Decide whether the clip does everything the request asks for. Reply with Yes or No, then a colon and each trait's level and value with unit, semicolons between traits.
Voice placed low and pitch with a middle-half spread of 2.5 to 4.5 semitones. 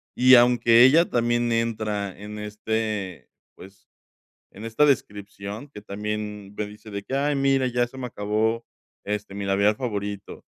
Yes: low, 105 Hz; average, 2.8 semitones